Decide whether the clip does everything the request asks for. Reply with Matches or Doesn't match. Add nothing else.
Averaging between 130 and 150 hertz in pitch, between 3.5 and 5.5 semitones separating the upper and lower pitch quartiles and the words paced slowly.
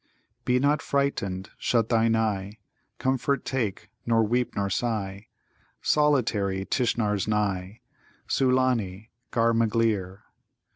Doesn't match